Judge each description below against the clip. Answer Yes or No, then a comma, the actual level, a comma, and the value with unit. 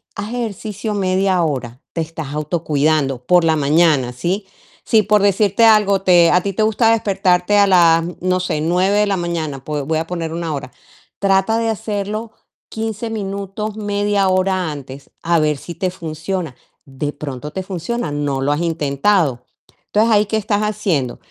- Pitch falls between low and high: Yes, medium, 180 Hz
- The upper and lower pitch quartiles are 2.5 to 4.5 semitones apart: No, average, 5.0 semitones